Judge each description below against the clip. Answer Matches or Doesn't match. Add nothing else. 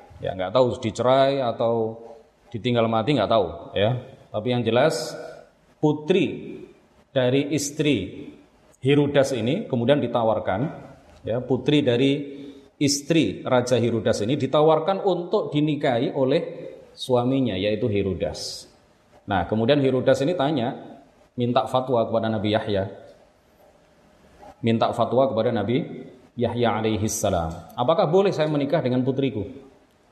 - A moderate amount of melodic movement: Matches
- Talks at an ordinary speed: Matches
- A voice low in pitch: Matches